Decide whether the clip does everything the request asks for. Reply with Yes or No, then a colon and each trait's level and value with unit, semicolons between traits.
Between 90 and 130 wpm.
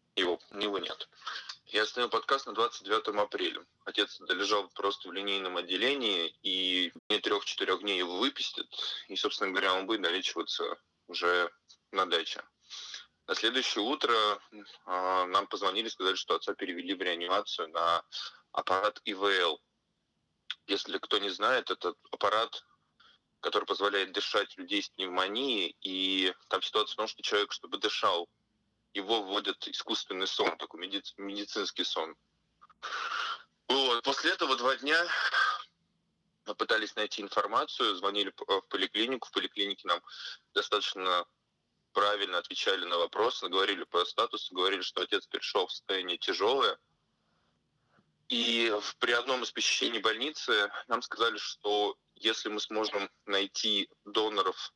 Yes: average, 125 wpm